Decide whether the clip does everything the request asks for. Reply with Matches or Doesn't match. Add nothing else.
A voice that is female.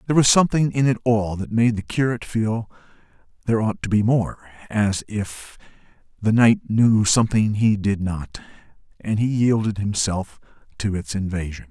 Doesn't match